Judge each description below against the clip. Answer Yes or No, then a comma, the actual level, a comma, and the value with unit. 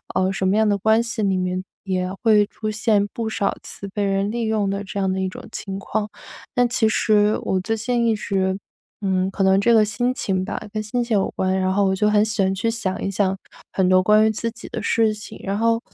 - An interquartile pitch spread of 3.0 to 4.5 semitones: No, narrow, 2.5 semitones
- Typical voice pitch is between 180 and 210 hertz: Yes, high, 205 Hz